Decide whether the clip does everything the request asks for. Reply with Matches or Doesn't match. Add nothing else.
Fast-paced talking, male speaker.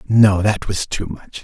Matches